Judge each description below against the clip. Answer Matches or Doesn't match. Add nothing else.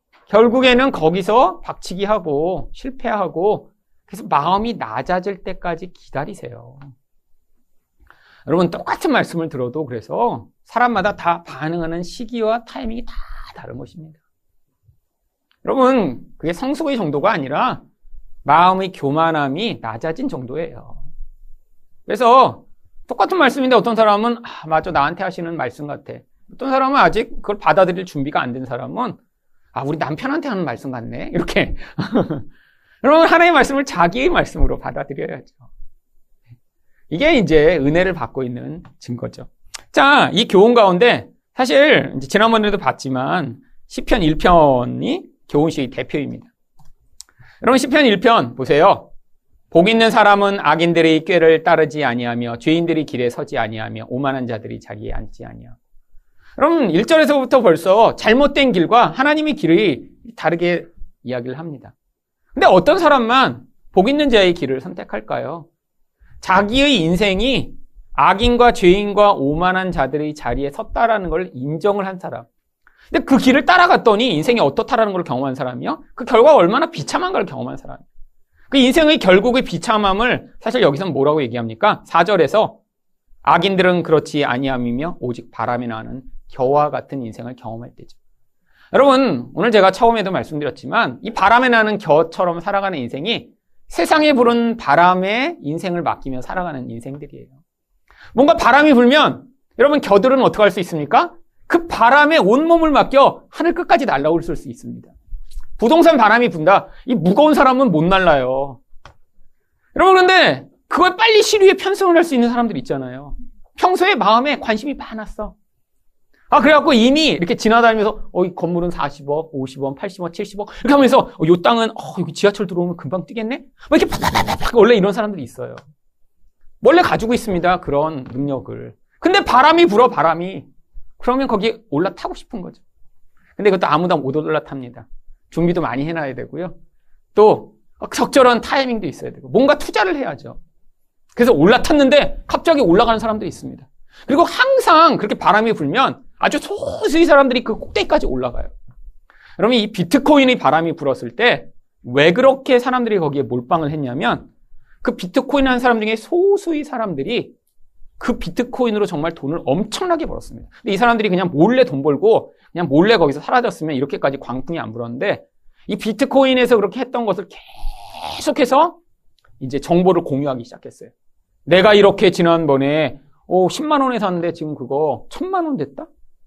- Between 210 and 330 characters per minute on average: Doesn't match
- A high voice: Matches